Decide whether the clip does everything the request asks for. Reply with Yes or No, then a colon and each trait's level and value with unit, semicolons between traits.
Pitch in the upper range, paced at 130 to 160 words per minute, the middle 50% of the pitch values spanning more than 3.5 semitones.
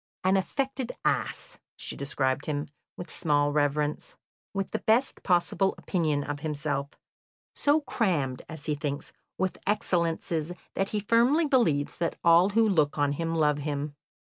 No: medium, 165 Hz; average, 150 wpm; average, 5.2 semitones